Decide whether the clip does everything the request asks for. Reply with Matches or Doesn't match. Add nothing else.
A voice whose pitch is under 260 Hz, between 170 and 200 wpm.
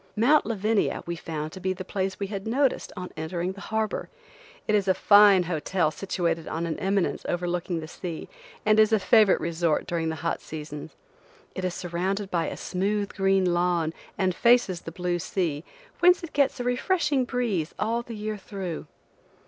Matches